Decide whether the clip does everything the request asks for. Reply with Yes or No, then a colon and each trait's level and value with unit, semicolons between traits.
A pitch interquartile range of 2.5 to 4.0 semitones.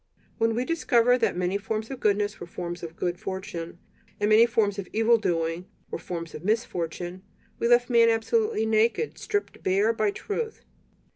No: average, 4.5 semitones